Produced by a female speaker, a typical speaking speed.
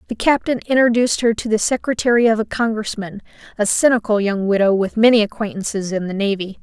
Yes: female; average, 180 wpm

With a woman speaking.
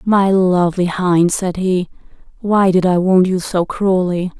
Yes: female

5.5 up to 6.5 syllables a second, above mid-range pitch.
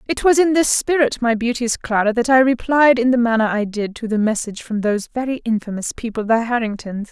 Yes: 5.8 syllables/s; high, 235 Hz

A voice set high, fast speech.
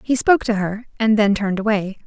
Yes: high, 215 Hz; fast, 230 wpm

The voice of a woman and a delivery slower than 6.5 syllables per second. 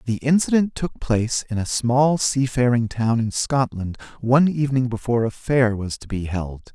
No: male; 5.0 syllables/s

